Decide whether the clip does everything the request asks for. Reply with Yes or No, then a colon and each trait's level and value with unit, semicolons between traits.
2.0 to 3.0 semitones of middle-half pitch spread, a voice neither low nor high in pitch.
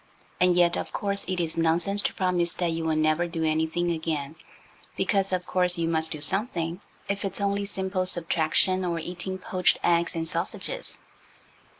Yes: narrow, 2.4 semitones; medium, 175 Hz